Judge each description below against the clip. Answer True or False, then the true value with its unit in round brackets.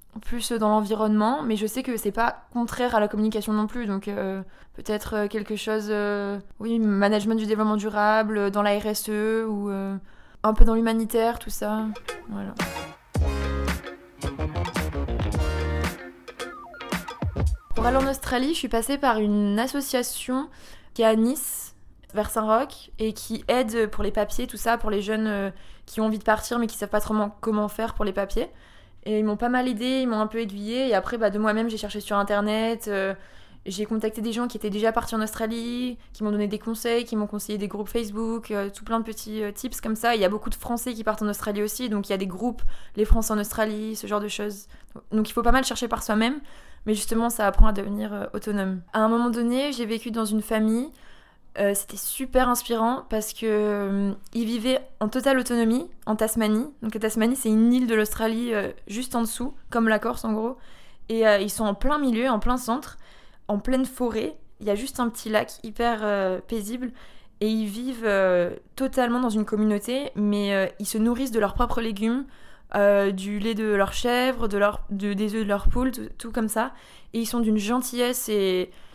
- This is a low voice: False (220 Hz)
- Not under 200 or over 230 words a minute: True (210 wpm)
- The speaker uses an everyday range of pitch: False (2.2 semitones)